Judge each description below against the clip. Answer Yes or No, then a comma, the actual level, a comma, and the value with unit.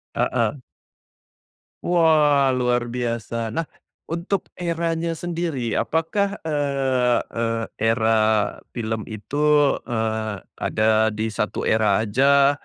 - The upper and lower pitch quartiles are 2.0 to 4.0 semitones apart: No, wide, 5.4 semitones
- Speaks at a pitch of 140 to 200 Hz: No, low, 125 Hz